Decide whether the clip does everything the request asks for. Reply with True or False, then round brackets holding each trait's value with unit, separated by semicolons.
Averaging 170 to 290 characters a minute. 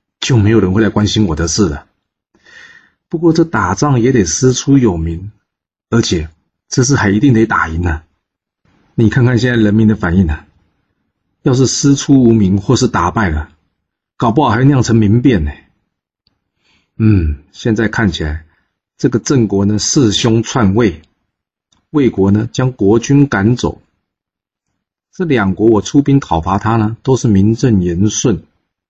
True (220 characters per minute)